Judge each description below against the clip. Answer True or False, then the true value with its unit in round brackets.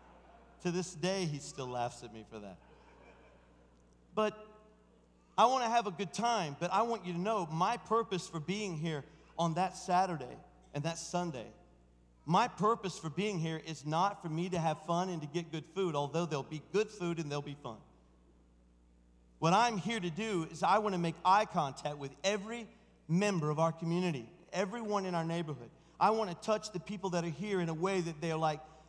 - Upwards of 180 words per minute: True (205 wpm)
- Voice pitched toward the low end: False (170 Hz)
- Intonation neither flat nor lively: True (4.5 semitones)